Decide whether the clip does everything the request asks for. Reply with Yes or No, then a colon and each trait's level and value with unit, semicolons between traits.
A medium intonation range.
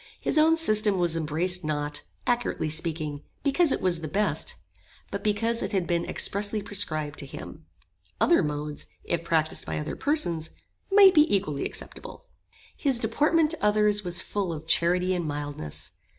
No: wide, 6.0 semitones